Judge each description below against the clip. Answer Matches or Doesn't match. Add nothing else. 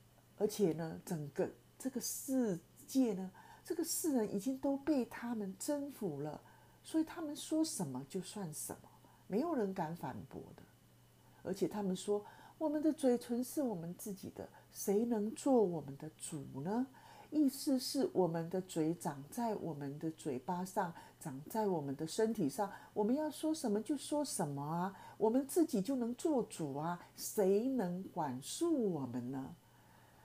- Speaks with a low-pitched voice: Doesn't match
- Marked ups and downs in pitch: Matches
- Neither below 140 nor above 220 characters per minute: Doesn't match